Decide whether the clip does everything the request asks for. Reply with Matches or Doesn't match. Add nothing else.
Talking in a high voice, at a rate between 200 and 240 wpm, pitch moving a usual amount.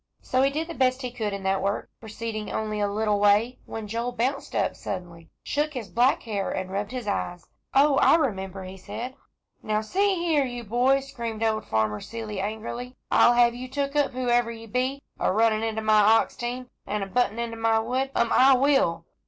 Matches